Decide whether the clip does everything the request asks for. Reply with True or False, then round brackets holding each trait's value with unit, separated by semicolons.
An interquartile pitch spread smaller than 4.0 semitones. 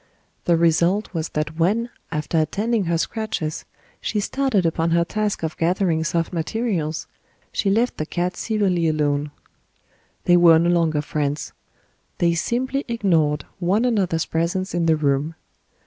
False (4.3 semitones)